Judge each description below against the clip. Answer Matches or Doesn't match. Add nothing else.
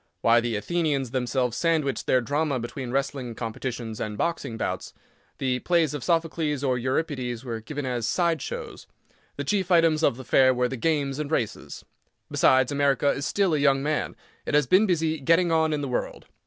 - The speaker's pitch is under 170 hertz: Matches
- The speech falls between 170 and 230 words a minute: Matches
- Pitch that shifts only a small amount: Doesn't match